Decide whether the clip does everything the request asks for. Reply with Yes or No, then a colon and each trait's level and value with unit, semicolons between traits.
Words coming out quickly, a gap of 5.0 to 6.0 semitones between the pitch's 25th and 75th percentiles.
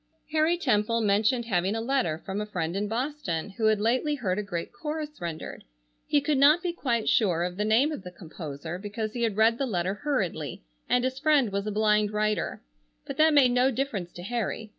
Yes: fast, 210 wpm; wide, 5.4 semitones